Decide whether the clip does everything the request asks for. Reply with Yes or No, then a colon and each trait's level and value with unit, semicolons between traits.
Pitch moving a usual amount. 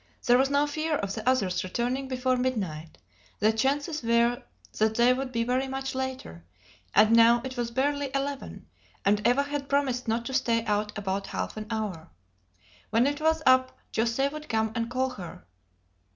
Yes: average, 3.5 semitones